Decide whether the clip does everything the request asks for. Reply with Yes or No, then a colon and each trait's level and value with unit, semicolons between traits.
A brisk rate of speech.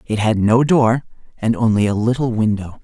No: average, 190 wpm